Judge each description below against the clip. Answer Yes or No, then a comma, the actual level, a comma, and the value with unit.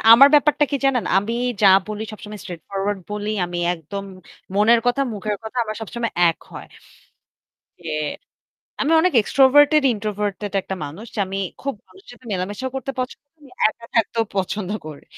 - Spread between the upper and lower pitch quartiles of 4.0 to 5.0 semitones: Yes, average, 4.7 semitones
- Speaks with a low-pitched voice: No, high, 215 Hz